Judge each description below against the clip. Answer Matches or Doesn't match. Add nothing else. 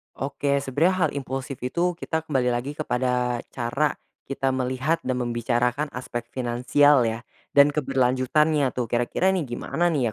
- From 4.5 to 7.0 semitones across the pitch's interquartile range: Doesn't match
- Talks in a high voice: Doesn't match